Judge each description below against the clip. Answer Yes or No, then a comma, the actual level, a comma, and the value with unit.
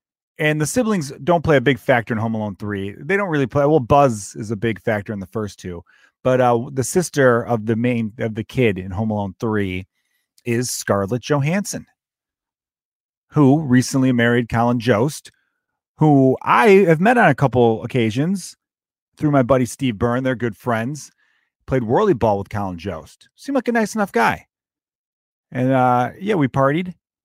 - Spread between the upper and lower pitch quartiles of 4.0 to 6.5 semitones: Yes, average, 4.3 semitones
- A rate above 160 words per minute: Yes, average, 180 wpm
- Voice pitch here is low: Yes, low, 125 Hz